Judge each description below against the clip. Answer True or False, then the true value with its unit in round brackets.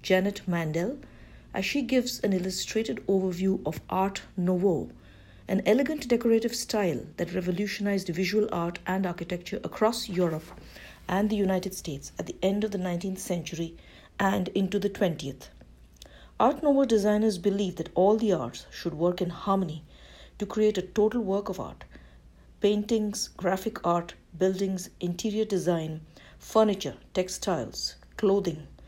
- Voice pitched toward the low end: False (190 Hz)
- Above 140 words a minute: False (135 wpm)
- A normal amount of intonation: True (3.3 semitones)